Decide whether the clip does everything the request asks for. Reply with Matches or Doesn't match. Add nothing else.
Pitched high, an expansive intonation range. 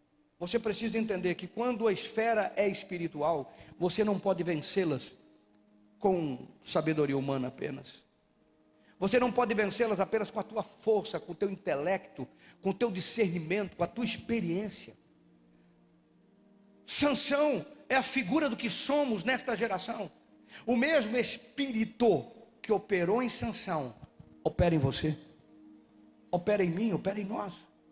Matches